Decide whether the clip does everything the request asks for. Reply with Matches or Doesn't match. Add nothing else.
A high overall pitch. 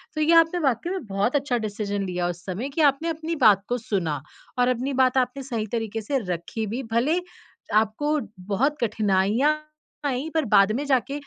Matches